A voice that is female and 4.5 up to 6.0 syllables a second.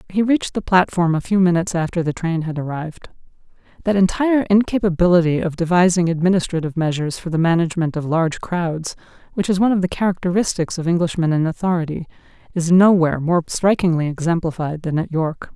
No: female; 6.4 syllables/s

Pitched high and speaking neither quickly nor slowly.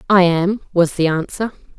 No: medium, 180 Hz; average, 170 wpm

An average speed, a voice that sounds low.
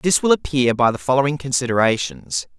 Yes: average, 165 wpm; low, 125 Hz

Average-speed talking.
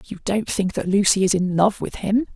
No: fast, 255 wpm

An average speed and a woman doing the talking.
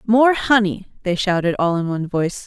Yes: average, 195 wpm; female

